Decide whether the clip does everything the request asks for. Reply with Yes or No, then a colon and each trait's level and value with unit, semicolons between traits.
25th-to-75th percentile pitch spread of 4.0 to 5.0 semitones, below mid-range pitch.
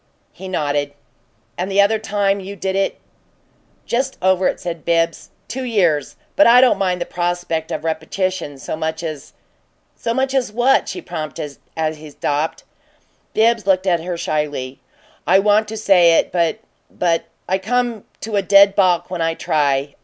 No: average, 4.4 semitones; medium, 185 Hz